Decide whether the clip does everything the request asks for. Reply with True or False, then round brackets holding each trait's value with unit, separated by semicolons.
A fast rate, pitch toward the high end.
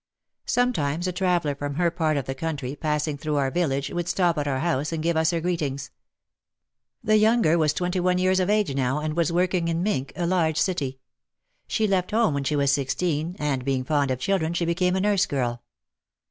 False (210 wpm; 160 Hz)